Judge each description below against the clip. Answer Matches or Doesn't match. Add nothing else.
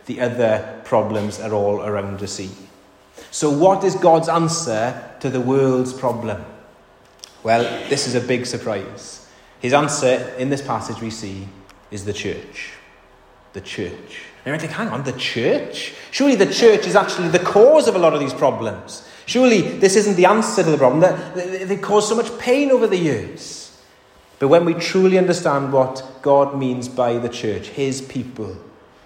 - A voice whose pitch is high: Doesn't match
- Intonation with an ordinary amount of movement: Doesn't match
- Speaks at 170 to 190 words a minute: Matches